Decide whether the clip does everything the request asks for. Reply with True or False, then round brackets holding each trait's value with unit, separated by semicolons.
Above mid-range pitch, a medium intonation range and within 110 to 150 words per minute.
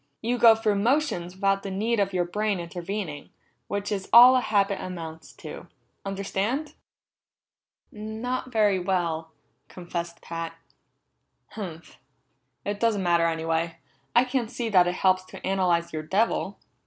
True (195 Hz; 4.1 semitones; 140 wpm)